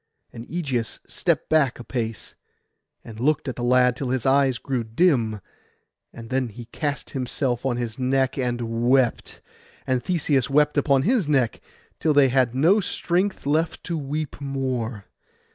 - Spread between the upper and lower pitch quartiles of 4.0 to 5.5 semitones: No, average, 3.2 semitones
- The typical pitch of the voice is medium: No, low, 130 Hz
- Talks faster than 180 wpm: No, average, 160 wpm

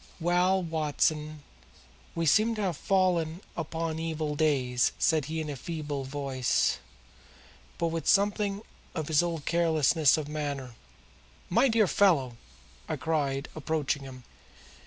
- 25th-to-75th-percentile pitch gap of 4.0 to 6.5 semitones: No, average, 3.0 semitones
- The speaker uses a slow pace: Yes, slow, 130 wpm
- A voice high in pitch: No, medium, 160 Hz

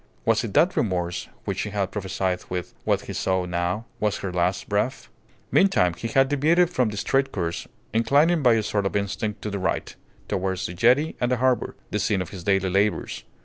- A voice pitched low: Yes, low, 100 Hz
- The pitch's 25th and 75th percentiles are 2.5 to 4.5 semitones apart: No, average, 4.9 semitones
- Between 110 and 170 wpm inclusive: No, fast, 205 wpm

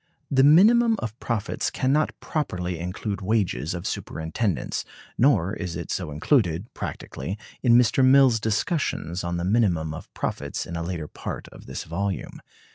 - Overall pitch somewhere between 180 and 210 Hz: No, low, 100 Hz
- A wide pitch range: Yes, wide, 6.7 semitones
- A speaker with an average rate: Yes, average, 155 wpm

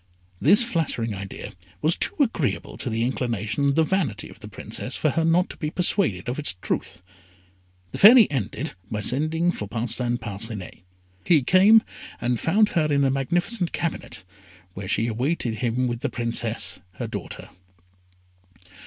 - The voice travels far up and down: Yes, wide, 6.7 semitones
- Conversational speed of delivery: Yes, average, 160 wpm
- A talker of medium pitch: No, low, 130 Hz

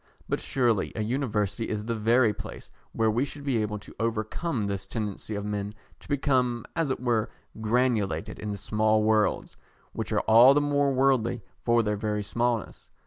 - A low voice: Yes, low, 110 Hz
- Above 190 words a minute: No, average, 175 wpm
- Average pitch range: Yes, average, 3.0 semitones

